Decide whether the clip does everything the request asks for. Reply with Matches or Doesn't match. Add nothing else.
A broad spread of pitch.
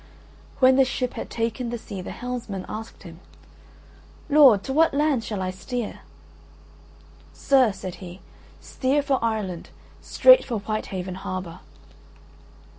Matches